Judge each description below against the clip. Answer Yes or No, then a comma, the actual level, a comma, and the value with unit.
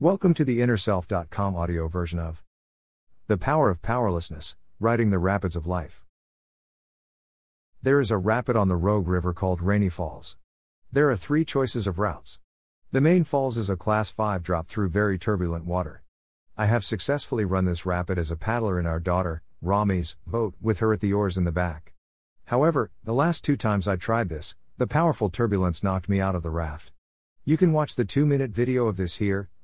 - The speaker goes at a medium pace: Yes, average, 190 wpm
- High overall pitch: No, low, 100 Hz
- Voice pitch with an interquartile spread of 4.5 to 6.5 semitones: Yes, average, 5.0 semitones